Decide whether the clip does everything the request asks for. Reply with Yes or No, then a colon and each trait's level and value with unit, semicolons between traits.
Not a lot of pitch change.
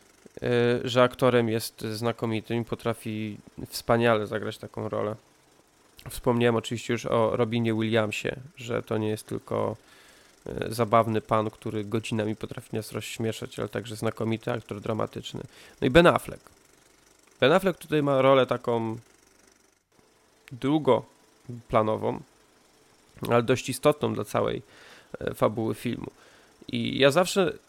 Yes: narrow, 2.0 semitones